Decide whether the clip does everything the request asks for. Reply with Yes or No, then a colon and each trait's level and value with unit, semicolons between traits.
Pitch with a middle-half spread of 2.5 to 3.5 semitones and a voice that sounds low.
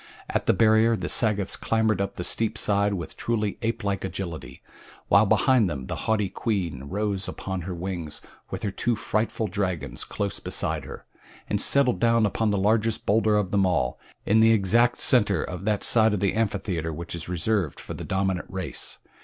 Yes: average, 3.2 semitones; low, 100 Hz